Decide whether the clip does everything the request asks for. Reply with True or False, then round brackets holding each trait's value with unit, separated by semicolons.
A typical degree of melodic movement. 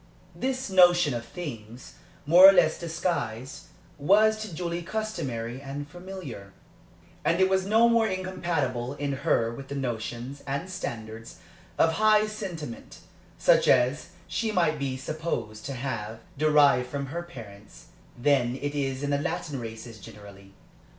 False (6.7 semitones)